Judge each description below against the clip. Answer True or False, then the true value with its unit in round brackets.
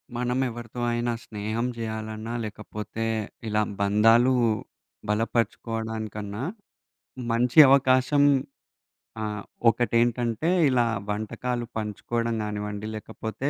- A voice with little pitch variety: True (2.0 semitones)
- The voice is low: True (115 Hz)